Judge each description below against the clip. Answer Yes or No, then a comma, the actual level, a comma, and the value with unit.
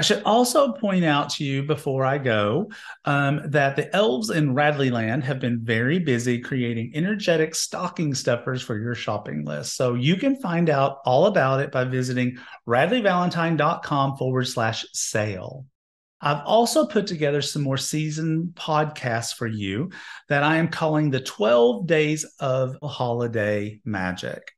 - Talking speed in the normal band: Yes, average, 150 wpm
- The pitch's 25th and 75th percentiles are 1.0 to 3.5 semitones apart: No, average, 4.8 semitones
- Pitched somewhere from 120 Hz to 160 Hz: Yes, medium, 140 Hz